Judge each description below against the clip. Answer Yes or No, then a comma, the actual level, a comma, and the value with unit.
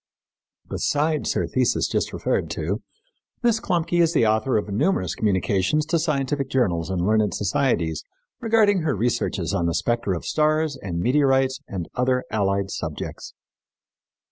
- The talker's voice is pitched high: No, low, 125 Hz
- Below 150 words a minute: Yes, average, 140 wpm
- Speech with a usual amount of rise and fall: No, wide, 7.8 semitones